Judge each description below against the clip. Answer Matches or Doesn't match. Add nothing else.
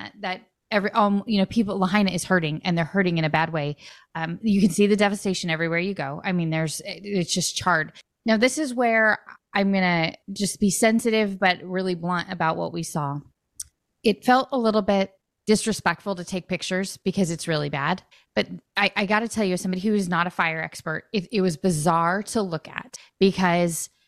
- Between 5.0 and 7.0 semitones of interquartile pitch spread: Doesn't match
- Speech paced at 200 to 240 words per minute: Matches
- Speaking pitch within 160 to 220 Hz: Matches